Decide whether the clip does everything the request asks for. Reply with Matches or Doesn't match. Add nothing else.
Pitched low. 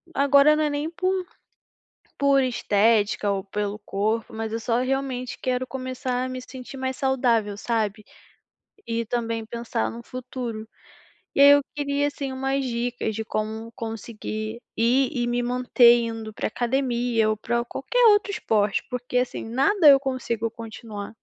Doesn't match